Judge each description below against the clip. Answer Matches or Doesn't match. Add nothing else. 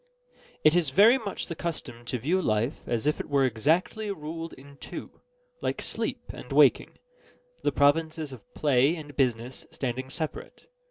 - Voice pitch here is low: Doesn't match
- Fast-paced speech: Doesn't match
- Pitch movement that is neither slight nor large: Matches